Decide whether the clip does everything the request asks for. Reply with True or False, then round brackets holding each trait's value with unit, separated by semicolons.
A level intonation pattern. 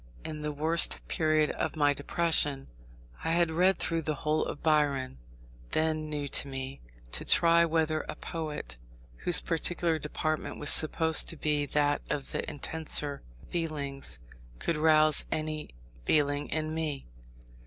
True (1.8 semitones)